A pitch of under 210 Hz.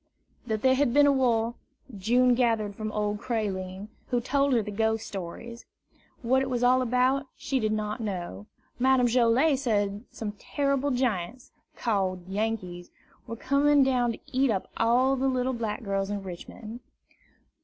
No: high, 230 Hz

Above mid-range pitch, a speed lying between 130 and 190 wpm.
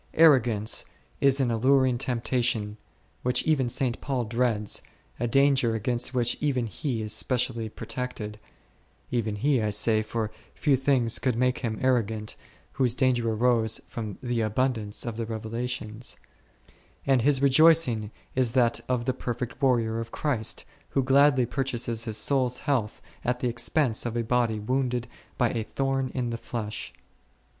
No: low, 120 Hz; average, 150 wpm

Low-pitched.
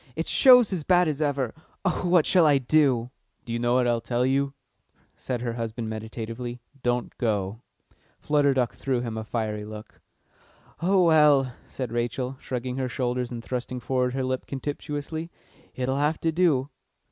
Yes: low, 130 Hz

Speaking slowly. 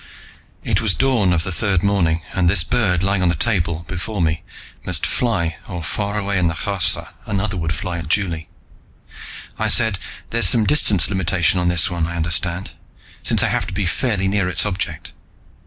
No: average, 190 wpm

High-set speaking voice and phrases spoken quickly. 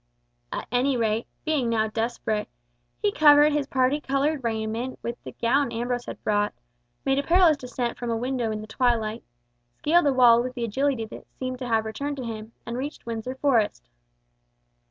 No: high, 245 Hz; average, 180 wpm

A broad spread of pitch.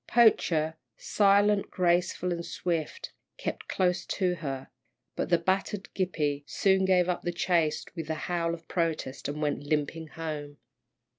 No: average, 3.1 semitones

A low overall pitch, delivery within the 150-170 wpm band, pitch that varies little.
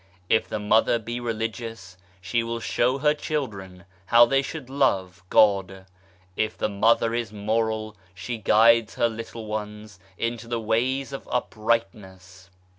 No: low, 110 Hz; average, 140 wpm; narrow, 2.2 semitones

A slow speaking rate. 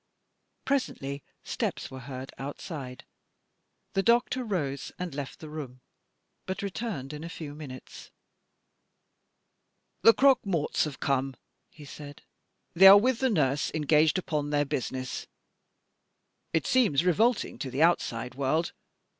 Yes: slow, 130 wpm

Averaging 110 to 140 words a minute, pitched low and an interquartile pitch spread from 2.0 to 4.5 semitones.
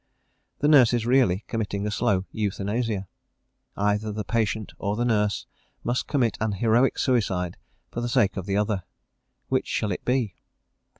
No: average, 160 wpm; low, 110 Hz; average, 3.0 semitones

